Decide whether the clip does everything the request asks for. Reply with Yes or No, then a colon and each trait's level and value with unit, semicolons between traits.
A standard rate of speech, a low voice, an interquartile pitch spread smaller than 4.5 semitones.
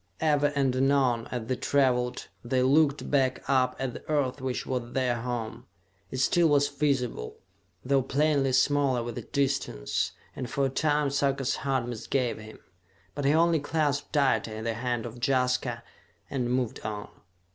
Yes: average, 155 wpm; low, 130 Hz; narrow, 2.5 semitones